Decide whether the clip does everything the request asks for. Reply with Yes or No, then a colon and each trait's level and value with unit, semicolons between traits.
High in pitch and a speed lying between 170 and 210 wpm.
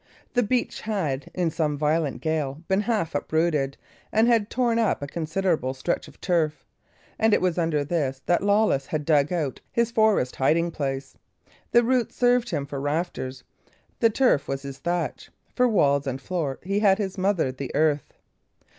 No: medium, 165 Hz; average, 175 wpm